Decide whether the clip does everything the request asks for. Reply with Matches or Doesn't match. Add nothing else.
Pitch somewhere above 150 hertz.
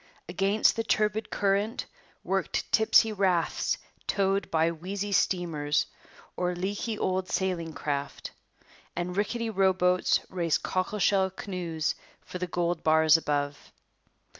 Matches